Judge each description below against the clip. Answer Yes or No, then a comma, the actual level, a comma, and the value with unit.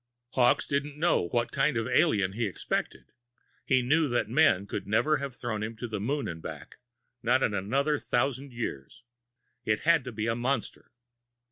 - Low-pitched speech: Yes, low, 120 Hz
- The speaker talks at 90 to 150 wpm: No, average, 180 wpm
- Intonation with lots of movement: No, average, 4.6 semitones